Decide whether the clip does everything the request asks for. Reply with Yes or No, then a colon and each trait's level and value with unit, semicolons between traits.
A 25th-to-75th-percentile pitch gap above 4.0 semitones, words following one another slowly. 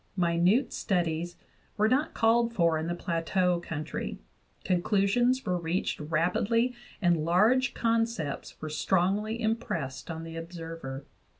Yes: average, 5.3 semitones; slow, 120 wpm